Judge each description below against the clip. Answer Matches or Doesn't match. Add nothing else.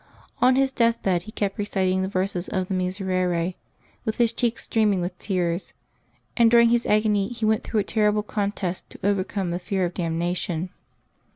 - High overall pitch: Matches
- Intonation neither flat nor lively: Matches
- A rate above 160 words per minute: Matches